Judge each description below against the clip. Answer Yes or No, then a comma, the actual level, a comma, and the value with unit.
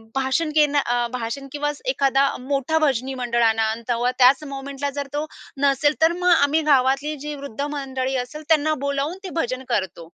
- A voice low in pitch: No, very high, 275 Hz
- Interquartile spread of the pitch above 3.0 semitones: No, average, 2.7 semitones